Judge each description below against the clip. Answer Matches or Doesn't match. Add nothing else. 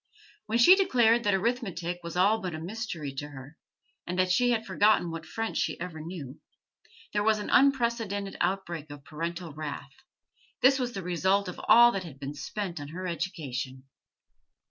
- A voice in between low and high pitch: Matches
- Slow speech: Doesn't match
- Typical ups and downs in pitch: Doesn't match